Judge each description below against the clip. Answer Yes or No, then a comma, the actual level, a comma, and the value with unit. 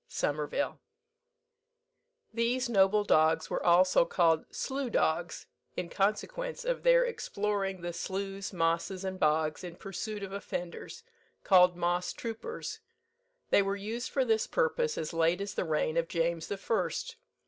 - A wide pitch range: No, average, 5.0 semitones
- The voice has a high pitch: Yes, high, 195 Hz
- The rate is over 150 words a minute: No, average, 140 wpm